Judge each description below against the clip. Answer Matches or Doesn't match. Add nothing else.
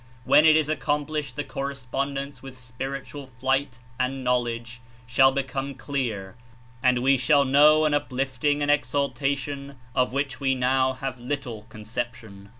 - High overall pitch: Doesn't match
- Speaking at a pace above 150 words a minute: Doesn't match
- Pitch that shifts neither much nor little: Doesn't match